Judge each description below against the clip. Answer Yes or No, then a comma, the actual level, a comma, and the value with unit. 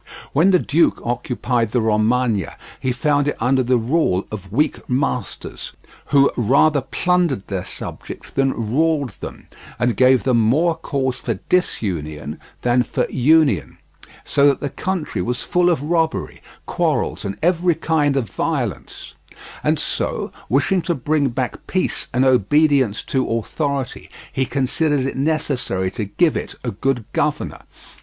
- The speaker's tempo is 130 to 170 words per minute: Yes, average, 145 wpm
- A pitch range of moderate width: Yes, average, 4.6 semitones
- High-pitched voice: No, low, 130 Hz